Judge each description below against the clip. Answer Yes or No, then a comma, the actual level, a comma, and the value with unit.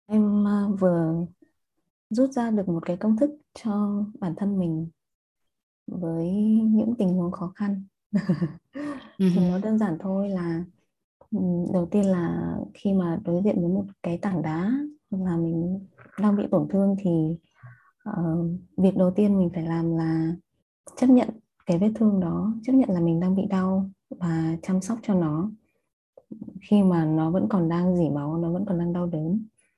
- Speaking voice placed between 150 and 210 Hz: Yes, high, 190 Hz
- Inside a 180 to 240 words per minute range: No, average, 170 wpm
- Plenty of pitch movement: No, average, 3.5 semitones